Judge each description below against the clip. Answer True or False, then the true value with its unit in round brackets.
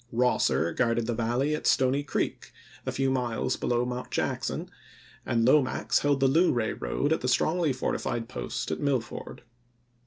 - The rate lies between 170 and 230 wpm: False (160 wpm)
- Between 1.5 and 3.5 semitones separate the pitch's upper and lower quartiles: True (3.0 semitones)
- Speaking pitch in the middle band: False (125 Hz)